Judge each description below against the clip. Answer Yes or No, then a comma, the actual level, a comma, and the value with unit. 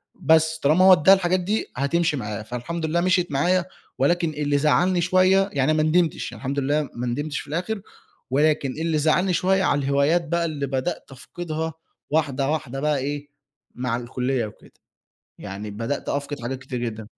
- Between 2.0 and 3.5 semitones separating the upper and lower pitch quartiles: No, average, 4.2 semitones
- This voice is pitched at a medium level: Yes, medium, 150 Hz